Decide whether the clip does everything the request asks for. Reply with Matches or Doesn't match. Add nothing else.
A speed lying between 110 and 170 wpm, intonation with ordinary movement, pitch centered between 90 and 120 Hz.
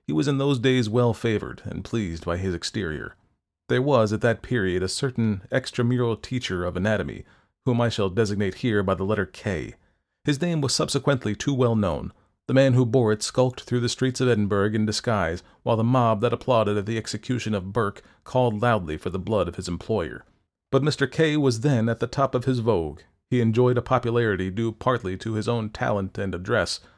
Doesn't match